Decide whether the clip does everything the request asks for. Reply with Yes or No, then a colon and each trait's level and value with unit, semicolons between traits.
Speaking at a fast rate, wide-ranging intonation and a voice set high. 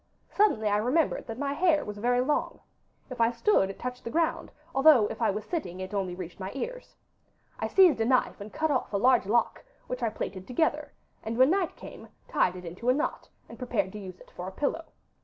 Yes: fast, 225 wpm; wide, 6.4 semitones; high, 240 Hz